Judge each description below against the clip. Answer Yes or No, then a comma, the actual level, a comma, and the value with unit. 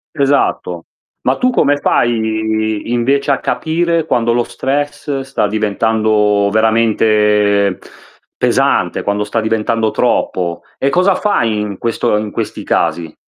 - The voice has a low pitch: Yes, low, 110 Hz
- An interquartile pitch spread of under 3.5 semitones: No, average, 4.4 semitones